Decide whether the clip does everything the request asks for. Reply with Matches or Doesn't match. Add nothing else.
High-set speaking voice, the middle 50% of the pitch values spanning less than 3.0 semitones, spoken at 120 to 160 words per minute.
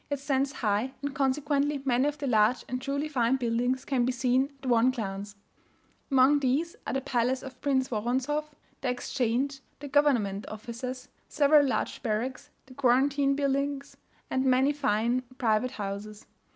Matches